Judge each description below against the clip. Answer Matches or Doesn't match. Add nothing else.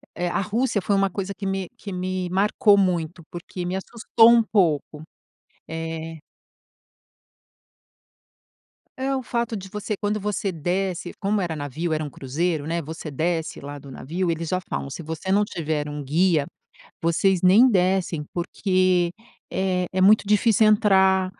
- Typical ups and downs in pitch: Matches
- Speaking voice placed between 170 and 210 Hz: Matches